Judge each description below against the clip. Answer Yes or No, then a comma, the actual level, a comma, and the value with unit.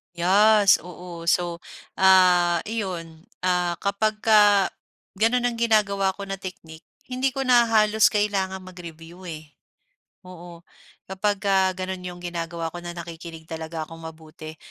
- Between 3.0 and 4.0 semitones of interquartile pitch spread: Yes, average, 3.4 semitones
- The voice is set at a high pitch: No, medium, 180 Hz